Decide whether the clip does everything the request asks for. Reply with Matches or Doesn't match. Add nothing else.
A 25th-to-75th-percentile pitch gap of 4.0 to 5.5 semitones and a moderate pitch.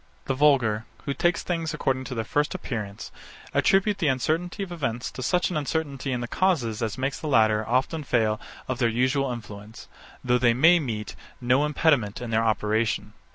Doesn't match